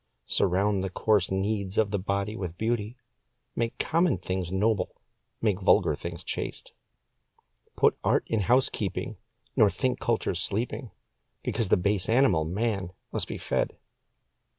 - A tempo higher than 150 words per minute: No, slow, 135 wpm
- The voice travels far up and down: No, average, 3.2 semitones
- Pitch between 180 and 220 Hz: No, low, 100 Hz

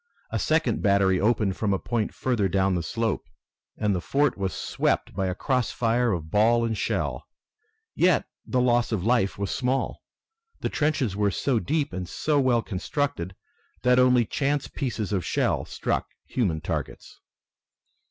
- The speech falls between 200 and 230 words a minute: No, average, 160 wpm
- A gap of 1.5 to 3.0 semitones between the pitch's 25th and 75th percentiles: No, average, 4.8 semitones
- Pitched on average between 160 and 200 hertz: No, low, 115 Hz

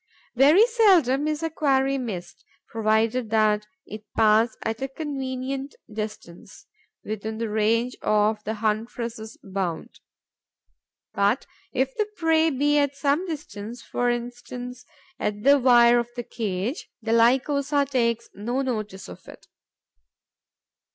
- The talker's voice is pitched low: No, high, 240 Hz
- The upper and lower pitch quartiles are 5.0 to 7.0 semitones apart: No, average, 4.1 semitones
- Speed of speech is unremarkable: No, slow, 125 wpm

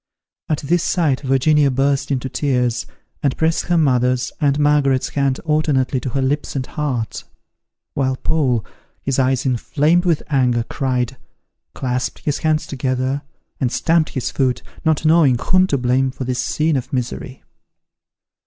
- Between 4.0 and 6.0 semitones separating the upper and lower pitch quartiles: No, average, 2.8 semitones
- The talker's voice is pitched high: No, low, 135 Hz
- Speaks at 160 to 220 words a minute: No, average, 150 wpm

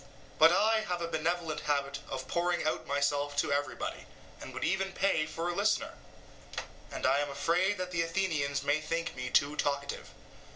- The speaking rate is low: No, average, 175 wpm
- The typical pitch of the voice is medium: Yes, medium, 155 Hz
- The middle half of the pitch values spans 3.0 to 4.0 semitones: Yes, average, 3.7 semitones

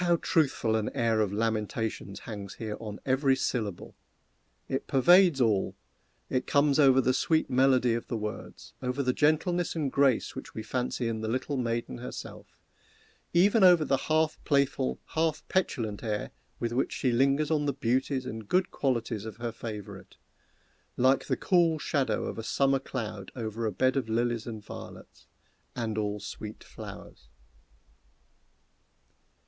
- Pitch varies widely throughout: No, average, 4.2 semitones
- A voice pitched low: Yes, low, 125 Hz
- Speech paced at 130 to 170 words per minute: Yes, average, 155 wpm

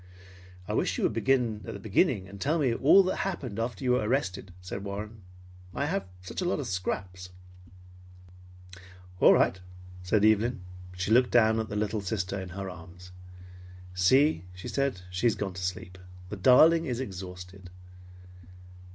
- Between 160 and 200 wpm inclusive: Yes, average, 170 wpm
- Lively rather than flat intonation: No, average, 4.9 semitones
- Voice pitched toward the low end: Yes, low, 100 Hz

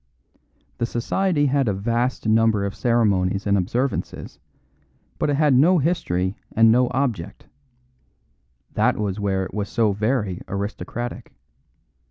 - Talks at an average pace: No, slow, 130 wpm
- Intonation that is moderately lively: Yes, average, 4.3 semitones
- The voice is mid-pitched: No, low, 110 Hz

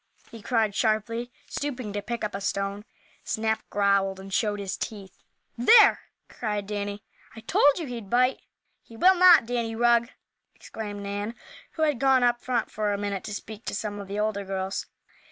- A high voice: Yes, high, 215 Hz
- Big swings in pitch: No, average, 3.0 semitones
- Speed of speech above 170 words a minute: Yes, average, 180 wpm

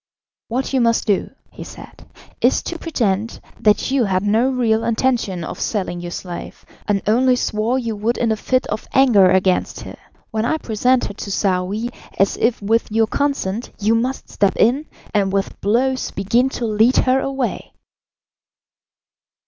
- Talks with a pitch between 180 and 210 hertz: No, high, 225 Hz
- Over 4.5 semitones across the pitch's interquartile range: No, average, 3.9 semitones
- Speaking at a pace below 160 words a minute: No, average, 165 wpm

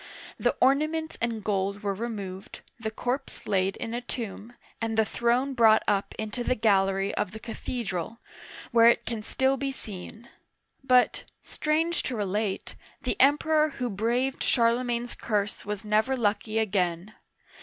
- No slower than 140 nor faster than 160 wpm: Yes, average, 150 wpm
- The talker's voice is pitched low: No, high, 225 Hz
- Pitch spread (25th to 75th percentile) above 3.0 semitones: Yes, average, 3.4 semitones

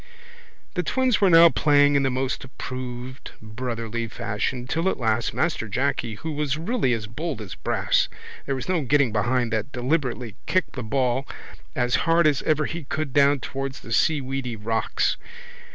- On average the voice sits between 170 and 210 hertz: No, low, 130 Hz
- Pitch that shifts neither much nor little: Yes, average, 4.2 semitones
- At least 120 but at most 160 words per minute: No, average, 170 wpm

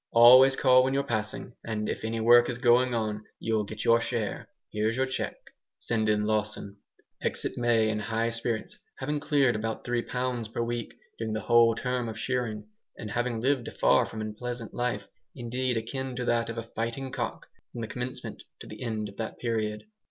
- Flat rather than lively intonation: Yes, narrow, 2.2 semitones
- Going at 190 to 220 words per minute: Yes, average, 195 wpm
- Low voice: Yes, low, 115 Hz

